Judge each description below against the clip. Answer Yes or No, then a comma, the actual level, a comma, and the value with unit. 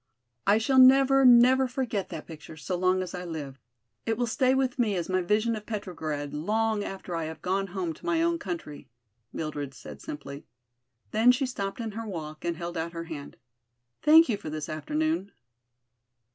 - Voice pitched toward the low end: No, high, 195 Hz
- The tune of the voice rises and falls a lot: Yes, wide, 7.0 semitones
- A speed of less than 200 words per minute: Yes, average, 185 wpm